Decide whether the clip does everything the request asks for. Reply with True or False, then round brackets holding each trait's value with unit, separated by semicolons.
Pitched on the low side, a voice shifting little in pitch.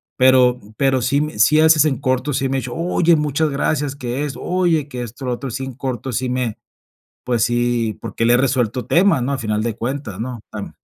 False (130 Hz; 3.1 semitones)